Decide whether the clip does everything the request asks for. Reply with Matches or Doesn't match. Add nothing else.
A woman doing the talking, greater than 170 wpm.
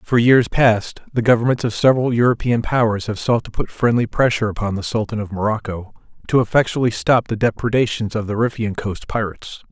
Doesn't match